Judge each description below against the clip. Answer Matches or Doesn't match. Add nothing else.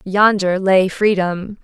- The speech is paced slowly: Matches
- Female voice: Matches